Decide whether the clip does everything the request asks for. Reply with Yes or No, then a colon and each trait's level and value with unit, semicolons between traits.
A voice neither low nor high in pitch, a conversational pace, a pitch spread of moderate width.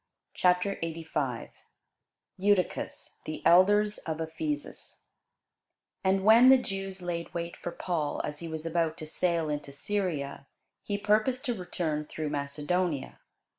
No: medium, 170 Hz; slow, 130 wpm; average, 3.9 semitones